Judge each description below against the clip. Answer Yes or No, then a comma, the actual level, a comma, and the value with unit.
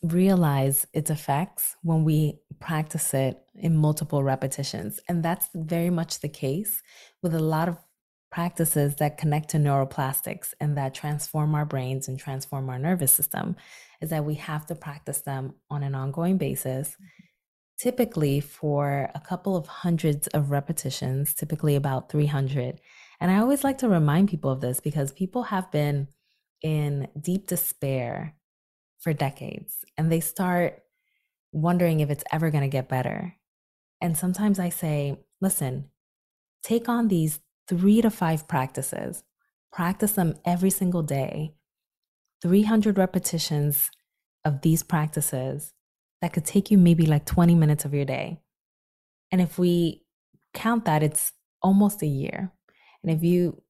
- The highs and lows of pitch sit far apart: No, average, 3.9 semitones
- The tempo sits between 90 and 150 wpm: Yes, average, 145 wpm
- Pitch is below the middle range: No, medium, 155 Hz